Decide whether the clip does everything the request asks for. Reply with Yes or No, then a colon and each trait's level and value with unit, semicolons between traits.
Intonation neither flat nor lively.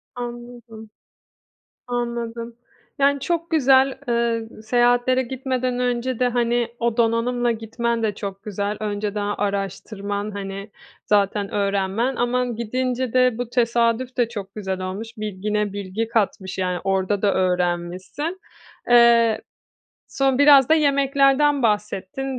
Yes: average, 3.5 semitones